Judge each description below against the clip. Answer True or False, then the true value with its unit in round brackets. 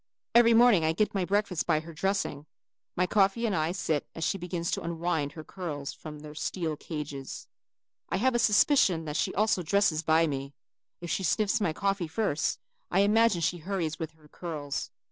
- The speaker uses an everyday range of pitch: True (4.3 semitones)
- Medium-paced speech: True (185 wpm)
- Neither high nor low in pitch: True (170 Hz)